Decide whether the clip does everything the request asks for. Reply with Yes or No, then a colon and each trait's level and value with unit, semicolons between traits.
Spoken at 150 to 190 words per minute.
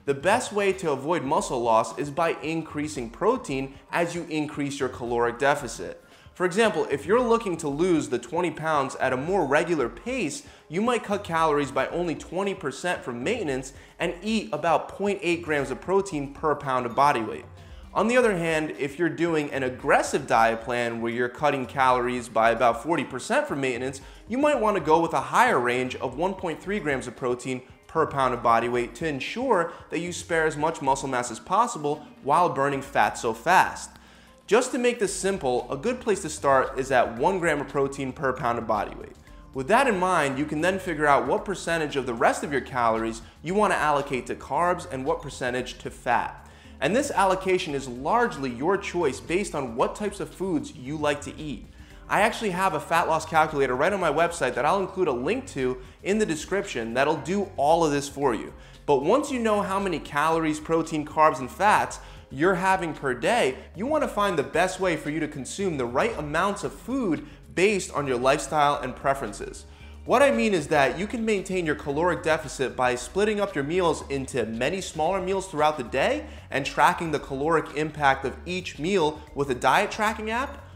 No: fast, 205 wpm